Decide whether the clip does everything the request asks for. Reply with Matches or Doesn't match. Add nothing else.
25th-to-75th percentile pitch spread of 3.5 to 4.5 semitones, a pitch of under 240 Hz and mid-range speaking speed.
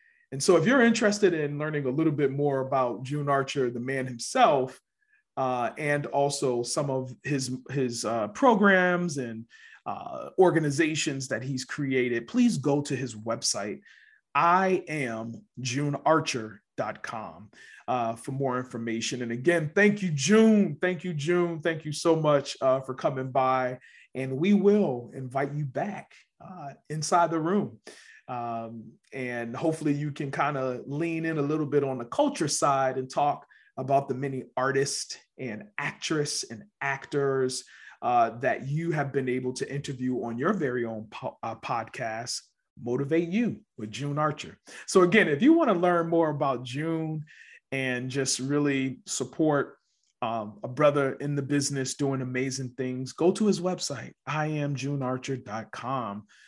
Matches